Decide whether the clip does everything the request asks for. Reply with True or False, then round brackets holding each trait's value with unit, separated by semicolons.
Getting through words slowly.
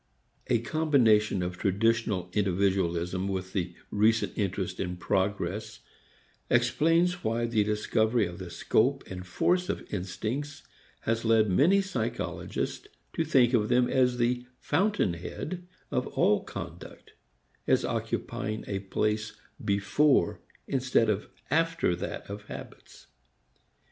True (120 wpm)